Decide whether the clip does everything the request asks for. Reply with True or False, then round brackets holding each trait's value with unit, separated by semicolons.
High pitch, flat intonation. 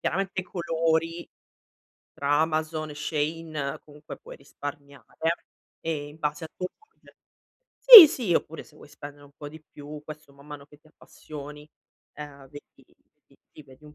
False (150 Hz; 1.8 semitones)